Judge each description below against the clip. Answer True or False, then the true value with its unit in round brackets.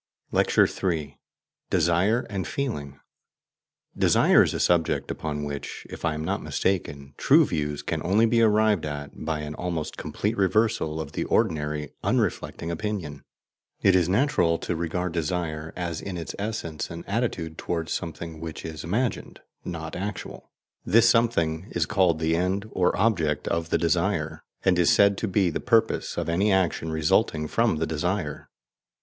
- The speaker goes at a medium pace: True (160 wpm)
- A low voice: True (85 Hz)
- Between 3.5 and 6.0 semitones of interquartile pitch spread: True (4.1 semitones)